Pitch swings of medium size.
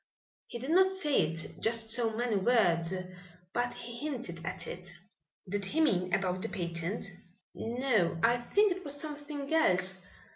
No: wide, 7.7 semitones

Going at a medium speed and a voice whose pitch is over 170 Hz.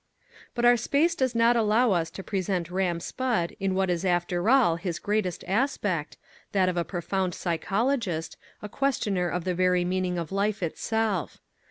Yes: average, 170 wpm; high, 190 Hz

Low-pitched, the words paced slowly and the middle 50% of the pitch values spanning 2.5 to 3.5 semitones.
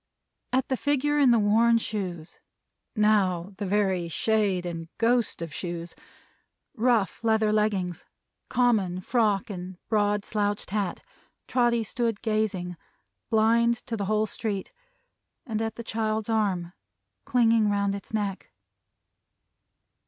No: high, 215 Hz; slow, 125 wpm; average, 3.0 semitones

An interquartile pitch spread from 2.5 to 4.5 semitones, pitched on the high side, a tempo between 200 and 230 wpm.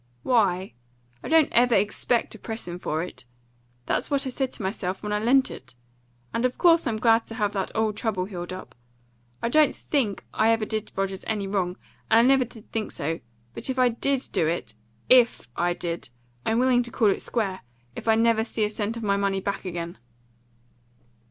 Yes: average, 3.9 semitones; high, 220 Hz; fast, 205 wpm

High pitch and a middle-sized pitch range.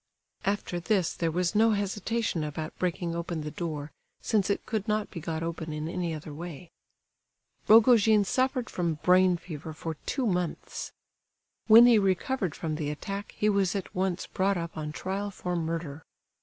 No: medium, 180 Hz; average, 4.0 semitones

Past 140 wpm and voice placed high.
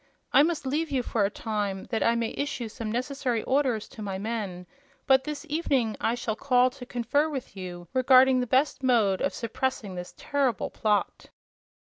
Yes: average, 180 wpm; high, 245 Hz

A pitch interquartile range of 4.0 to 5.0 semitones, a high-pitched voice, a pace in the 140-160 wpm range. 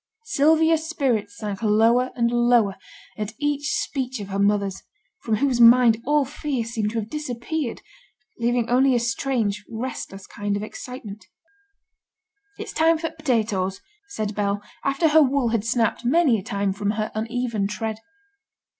Yes: average, 4.6 semitones; high, 235 Hz; average, 155 wpm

